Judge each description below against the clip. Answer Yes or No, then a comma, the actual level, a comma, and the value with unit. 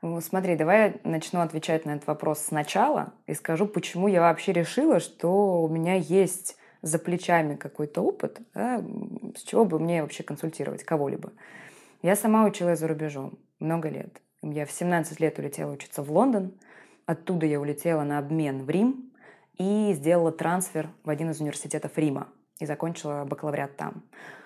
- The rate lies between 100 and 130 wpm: No, fast, 160 wpm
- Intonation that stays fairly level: No, average, 3.7 semitones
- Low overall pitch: No, medium, 165 Hz